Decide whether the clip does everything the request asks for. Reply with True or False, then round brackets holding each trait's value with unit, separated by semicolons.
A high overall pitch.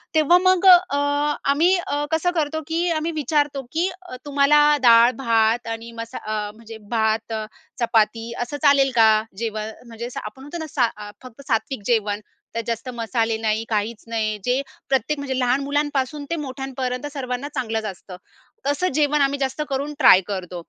True (255 Hz)